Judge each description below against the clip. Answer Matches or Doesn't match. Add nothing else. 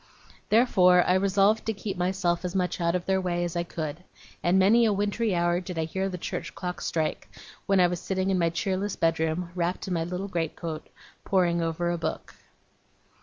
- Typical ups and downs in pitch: Doesn't match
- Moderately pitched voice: Matches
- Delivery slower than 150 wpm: Doesn't match